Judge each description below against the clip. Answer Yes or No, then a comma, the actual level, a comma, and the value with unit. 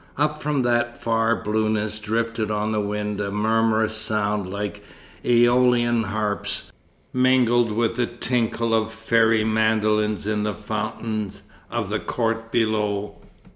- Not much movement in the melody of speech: Yes, narrow, 1.8 semitones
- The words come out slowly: Yes, slow, 130 wpm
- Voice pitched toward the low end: Yes, low, 110 Hz